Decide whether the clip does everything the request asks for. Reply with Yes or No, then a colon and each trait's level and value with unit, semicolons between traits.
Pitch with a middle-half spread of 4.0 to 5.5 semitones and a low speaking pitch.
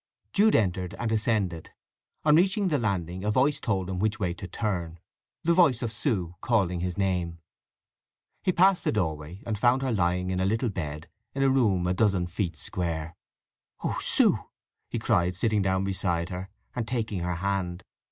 Yes: average, 4.5 semitones; very low, 95 Hz